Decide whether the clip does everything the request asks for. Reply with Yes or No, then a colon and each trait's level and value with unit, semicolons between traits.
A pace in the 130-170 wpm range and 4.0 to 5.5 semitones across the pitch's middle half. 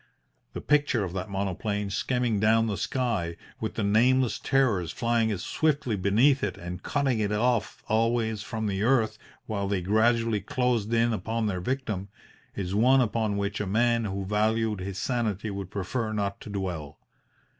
No: average, 165 wpm; average, 3.0 semitones